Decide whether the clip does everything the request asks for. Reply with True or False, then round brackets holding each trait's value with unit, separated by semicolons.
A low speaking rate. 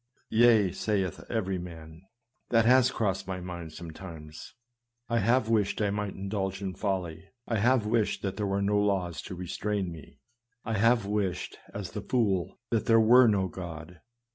False (170 wpm)